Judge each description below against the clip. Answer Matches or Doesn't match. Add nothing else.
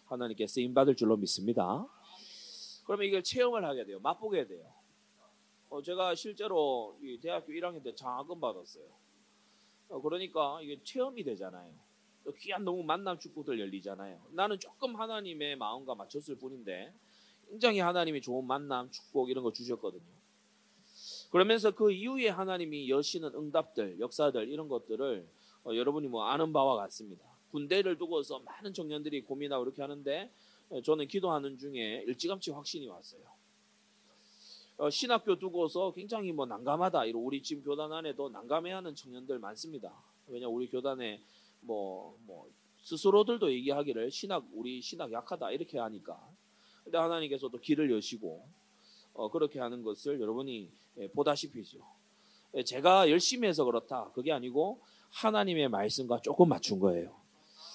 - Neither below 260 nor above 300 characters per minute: Doesn't match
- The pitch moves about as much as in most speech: Doesn't match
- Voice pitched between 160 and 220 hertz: Doesn't match